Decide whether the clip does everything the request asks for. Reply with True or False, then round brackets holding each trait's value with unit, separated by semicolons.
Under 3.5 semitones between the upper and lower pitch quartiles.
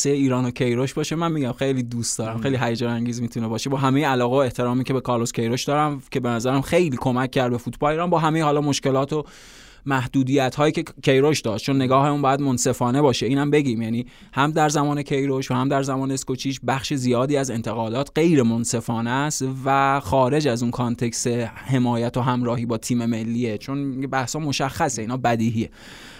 True (2.7 semitones)